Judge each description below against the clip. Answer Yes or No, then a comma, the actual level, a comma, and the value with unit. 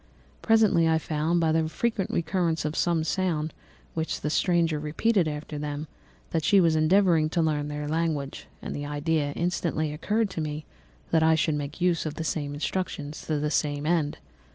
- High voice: No, medium, 160 Hz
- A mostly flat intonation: Yes, narrow, 2.3 semitones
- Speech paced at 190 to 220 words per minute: No, average, 180 wpm